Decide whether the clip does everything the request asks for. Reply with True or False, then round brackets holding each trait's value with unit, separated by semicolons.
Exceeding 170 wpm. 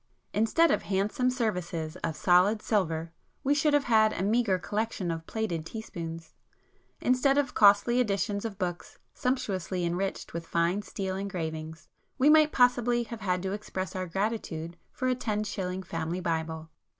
False (155 wpm)